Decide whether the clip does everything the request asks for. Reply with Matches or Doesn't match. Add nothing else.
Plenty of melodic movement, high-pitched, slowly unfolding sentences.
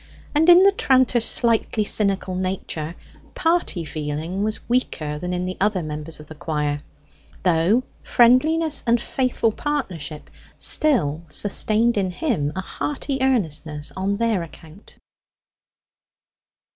Matches